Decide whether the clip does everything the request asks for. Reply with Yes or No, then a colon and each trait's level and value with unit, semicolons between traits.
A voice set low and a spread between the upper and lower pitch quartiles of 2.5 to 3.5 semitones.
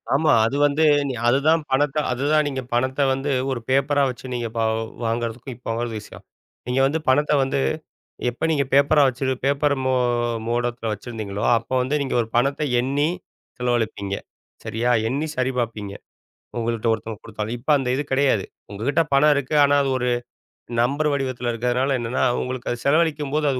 Yes: low, 130 Hz; average, 3.1 semitones